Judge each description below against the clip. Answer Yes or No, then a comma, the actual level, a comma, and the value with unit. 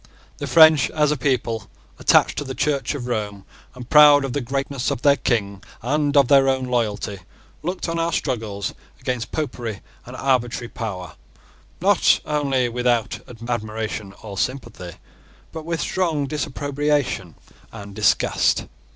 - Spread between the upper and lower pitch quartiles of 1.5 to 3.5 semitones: No, average, 4.6 semitones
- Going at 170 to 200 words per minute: No, average, 140 wpm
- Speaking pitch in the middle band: No, low, 130 Hz